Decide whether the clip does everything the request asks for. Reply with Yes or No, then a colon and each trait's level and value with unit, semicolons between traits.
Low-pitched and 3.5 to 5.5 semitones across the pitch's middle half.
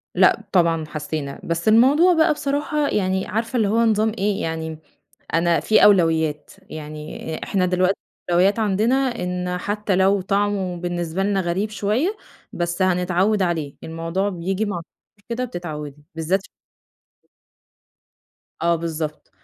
No: medium, 185 Hz; average, 4.0 semitones